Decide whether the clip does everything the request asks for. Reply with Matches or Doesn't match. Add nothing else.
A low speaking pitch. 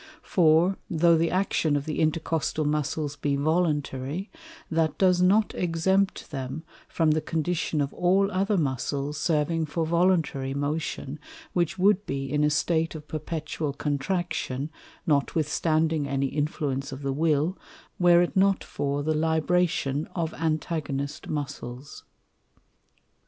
Doesn't match